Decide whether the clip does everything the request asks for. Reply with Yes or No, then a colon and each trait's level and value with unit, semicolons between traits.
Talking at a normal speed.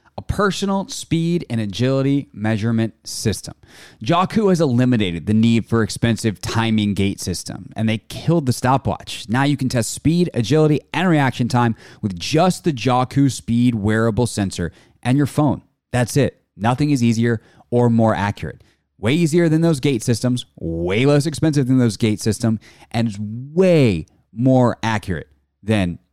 Yes: average, 155 wpm